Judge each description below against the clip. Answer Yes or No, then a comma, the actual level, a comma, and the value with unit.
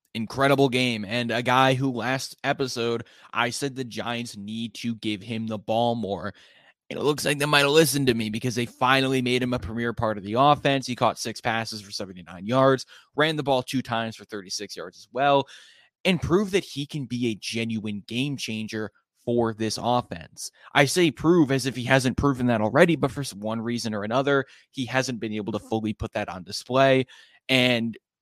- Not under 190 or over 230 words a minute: Yes, fast, 205 wpm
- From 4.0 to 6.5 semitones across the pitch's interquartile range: No, average, 3.4 semitones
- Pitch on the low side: Yes, low, 120 Hz